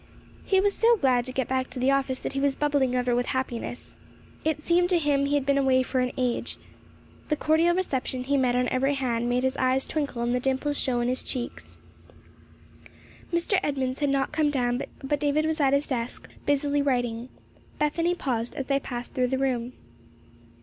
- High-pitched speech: Yes, very high, 270 Hz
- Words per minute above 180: Yes, average, 200 wpm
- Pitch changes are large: No, narrow, 2.6 semitones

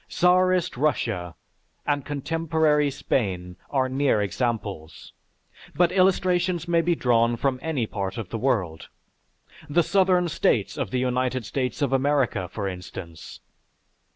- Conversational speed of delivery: No, slow, 125 wpm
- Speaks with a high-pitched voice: No, low, 130 Hz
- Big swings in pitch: Yes, wide, 6.7 semitones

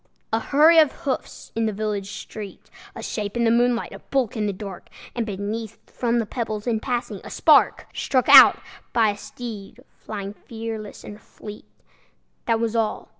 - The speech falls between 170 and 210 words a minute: Yes, average, 175 wpm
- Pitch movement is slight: Yes, narrow, 2.3 semitones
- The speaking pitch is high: Yes, high, 225 Hz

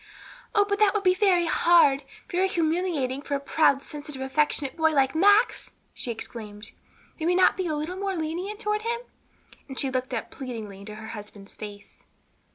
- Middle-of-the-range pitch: No, very high, 310 Hz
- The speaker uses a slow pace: No, average, 175 wpm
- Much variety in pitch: Yes, wide, 6.1 semitones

